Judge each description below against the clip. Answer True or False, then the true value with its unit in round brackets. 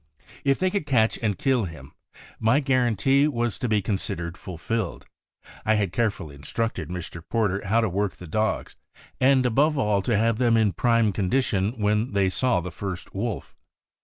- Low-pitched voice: True (110 Hz)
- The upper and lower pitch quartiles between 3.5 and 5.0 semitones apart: True (4.1 semitones)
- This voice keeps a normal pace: True (170 wpm)